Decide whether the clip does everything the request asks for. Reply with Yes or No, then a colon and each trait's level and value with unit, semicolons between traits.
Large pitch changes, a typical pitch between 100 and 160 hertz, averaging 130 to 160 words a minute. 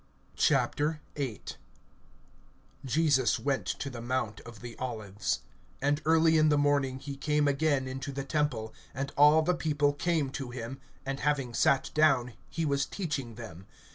No: average, 2.9 semitones; medium, 140 Hz; average, 150 wpm